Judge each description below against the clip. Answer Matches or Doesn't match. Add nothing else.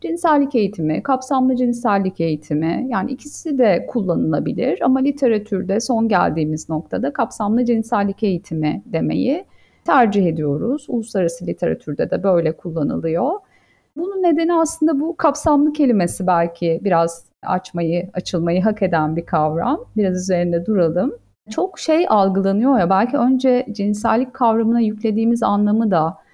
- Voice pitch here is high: Matches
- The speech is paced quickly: Doesn't match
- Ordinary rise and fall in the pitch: Doesn't match